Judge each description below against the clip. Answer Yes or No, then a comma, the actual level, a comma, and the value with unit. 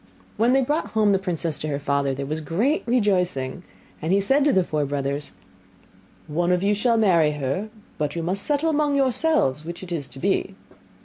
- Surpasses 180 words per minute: Yes, fast, 205 wpm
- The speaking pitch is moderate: Yes, medium, 180 Hz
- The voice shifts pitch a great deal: Yes, wide, 7.6 semitones